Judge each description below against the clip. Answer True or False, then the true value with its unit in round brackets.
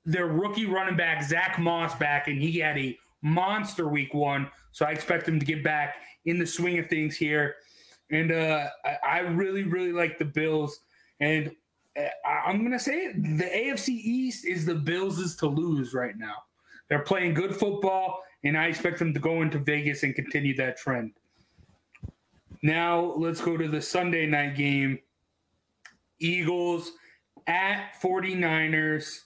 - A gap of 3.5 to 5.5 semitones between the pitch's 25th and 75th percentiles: False (3.0 semitones)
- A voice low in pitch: False (165 Hz)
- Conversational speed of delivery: True (165 wpm)